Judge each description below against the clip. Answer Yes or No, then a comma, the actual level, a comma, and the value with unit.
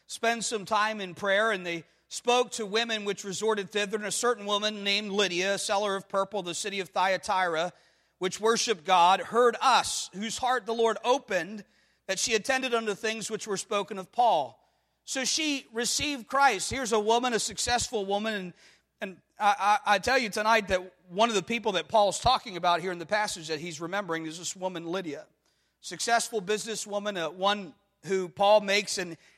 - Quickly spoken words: No, average, 190 wpm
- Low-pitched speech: No, high, 205 Hz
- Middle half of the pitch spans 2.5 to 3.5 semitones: Yes, average, 3.0 semitones